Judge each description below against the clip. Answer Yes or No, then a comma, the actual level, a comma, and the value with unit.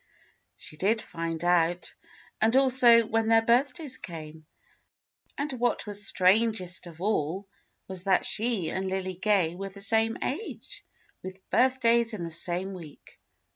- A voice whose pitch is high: Yes, high, 195 Hz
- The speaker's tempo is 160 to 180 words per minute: No, average, 140 wpm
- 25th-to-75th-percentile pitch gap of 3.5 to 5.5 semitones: Yes, average, 4.7 semitones